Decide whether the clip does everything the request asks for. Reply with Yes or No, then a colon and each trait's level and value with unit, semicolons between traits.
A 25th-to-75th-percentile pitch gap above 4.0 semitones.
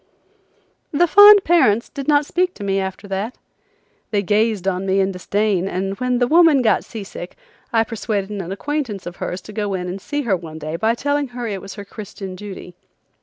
Yes: average, 4.6 semitones